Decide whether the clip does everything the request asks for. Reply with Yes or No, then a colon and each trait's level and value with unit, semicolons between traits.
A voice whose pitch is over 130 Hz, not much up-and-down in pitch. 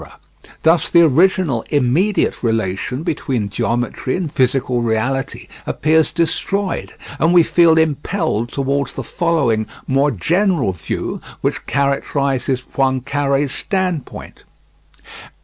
No: medium, 140 Hz; average, 4.8 semitones